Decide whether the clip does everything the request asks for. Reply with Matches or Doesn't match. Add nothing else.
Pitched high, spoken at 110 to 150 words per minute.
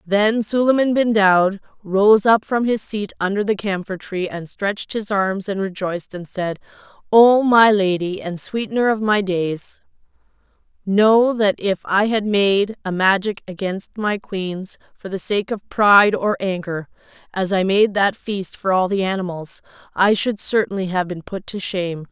Doesn't match